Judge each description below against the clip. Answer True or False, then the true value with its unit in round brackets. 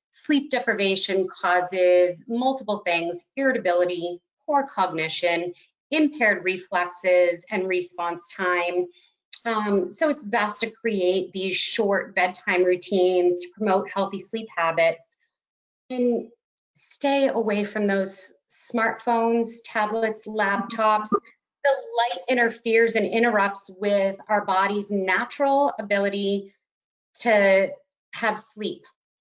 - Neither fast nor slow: False (100 wpm)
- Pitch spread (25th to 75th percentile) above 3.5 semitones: True (4.0 semitones)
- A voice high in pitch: True (200 Hz)